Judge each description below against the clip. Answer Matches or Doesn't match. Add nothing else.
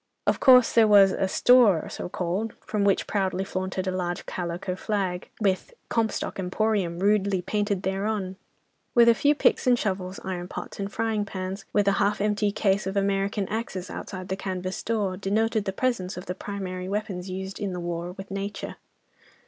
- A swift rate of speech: Doesn't match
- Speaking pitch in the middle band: Doesn't match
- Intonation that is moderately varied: Doesn't match